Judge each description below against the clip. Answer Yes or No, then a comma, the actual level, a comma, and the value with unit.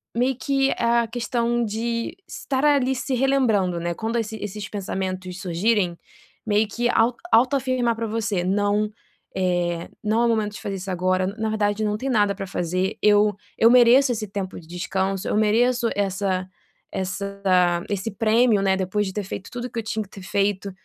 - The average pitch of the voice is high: Yes, high, 210 Hz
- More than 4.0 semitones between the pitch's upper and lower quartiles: No, average, 3.5 semitones